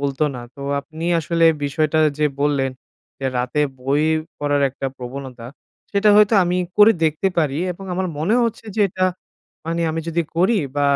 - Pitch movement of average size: Yes, average, 4.2 semitones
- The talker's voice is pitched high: No, medium, 155 Hz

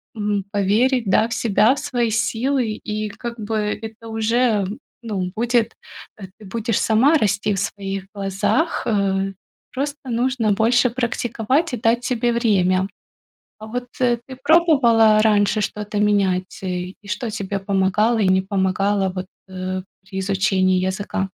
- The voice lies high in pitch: Yes, high, 215 Hz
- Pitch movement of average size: Yes, average, 3.3 semitones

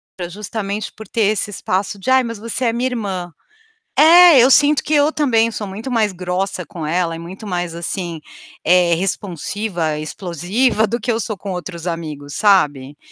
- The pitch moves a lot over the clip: No, average, 4.8 semitones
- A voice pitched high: Yes, high, 195 Hz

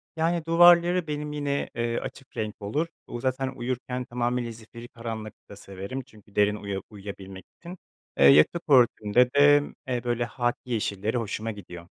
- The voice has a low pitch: Yes, low, 120 Hz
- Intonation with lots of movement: No, average, 5.0 semitones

